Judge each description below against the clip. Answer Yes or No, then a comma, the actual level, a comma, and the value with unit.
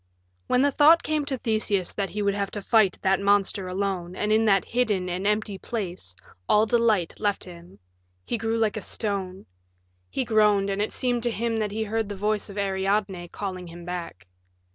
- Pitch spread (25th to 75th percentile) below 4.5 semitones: Yes, narrow, 2.6 semitones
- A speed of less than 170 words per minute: No, average, 195 wpm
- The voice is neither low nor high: No, high, 205 Hz